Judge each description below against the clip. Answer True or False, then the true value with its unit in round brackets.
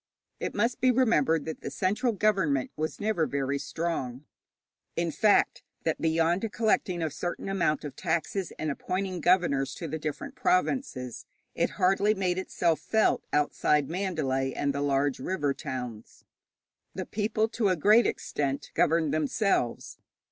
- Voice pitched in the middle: True (165 Hz)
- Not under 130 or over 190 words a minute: True (145 wpm)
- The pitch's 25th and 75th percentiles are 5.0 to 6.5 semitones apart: True (5.4 semitones)